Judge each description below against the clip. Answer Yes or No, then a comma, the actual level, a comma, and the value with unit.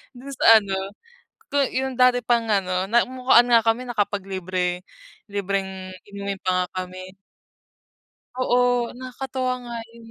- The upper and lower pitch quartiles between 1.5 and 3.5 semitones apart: No, average, 4.6 semitones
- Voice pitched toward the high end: Yes, high, 220 Hz